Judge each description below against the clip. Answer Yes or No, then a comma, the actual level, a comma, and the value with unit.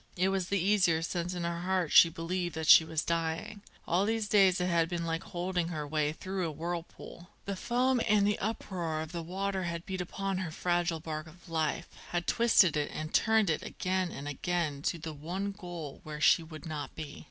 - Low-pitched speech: No, medium, 175 Hz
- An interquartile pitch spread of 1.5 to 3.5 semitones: Yes, average, 2.9 semitones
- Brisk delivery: Yes, fast, 210 wpm